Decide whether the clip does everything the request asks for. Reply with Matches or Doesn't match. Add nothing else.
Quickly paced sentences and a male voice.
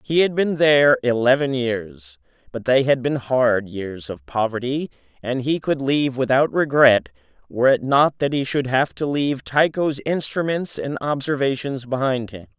Doesn't match